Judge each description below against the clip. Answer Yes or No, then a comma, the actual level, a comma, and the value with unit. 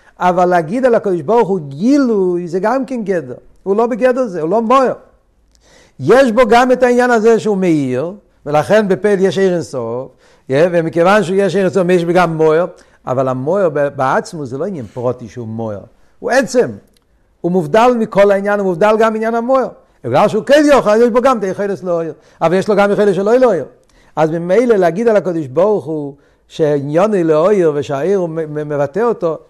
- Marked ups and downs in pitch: Yes, wide, 5.7 semitones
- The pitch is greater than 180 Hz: Yes, high, 190 Hz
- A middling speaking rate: No, fast, 185 wpm